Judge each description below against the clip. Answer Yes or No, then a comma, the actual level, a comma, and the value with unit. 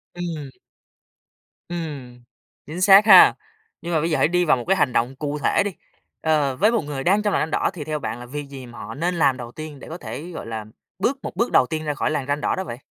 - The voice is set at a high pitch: No, medium, 150 Hz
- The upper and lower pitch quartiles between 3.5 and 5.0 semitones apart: Yes, average, 4.6 semitones